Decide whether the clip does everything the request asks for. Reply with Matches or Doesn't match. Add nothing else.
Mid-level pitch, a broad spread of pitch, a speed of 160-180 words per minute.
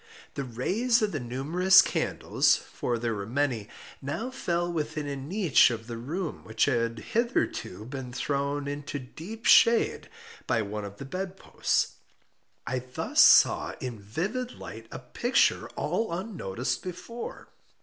Doesn't match